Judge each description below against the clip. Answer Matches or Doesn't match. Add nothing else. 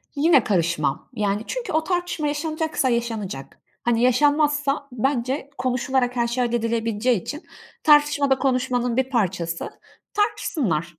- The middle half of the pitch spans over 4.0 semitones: Matches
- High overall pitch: Matches